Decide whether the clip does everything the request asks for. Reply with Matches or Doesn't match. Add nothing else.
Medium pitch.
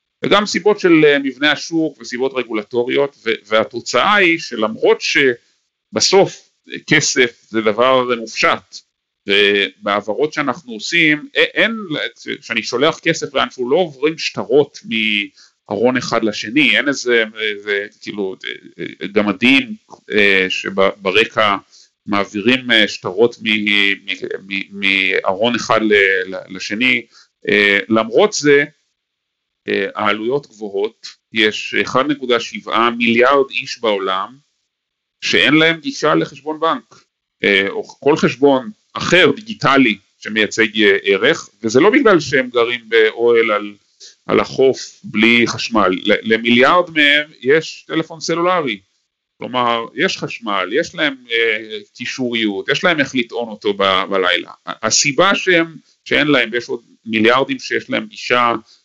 Doesn't match